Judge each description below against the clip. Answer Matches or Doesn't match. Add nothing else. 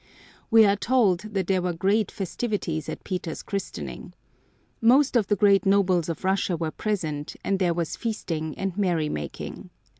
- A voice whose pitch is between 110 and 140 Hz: Doesn't match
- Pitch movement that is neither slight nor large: Matches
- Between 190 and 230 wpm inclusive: Doesn't match